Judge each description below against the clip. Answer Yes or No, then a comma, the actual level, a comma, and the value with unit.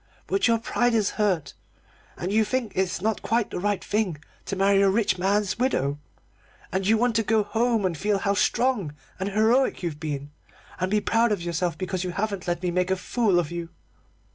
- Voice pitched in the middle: No, high, 200 Hz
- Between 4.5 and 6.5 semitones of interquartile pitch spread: No, average, 3.5 semitones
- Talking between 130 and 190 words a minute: No, fast, 205 wpm